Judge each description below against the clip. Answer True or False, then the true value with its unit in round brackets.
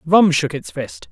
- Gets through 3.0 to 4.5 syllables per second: True (4.0 syllables/s)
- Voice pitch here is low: False (165 Hz)